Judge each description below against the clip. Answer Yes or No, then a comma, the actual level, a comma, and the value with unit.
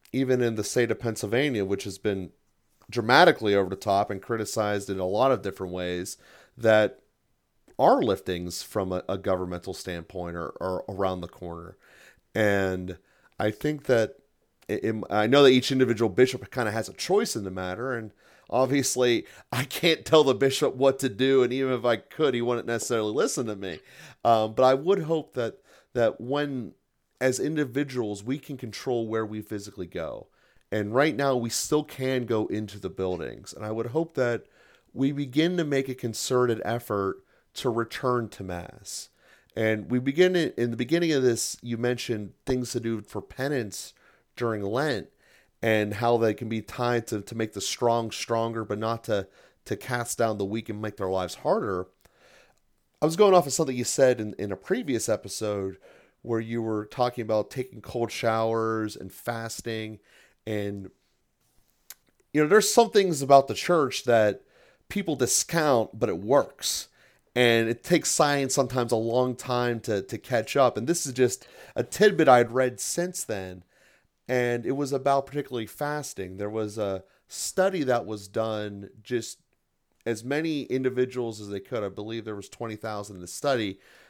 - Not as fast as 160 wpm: No, average, 175 wpm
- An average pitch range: Yes, average, 3.9 semitones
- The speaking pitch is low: Yes, low, 115 Hz